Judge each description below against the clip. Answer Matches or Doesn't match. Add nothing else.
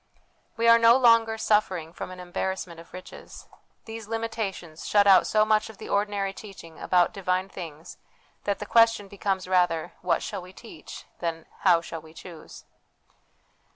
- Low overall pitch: Doesn't match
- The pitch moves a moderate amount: Matches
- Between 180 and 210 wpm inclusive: Doesn't match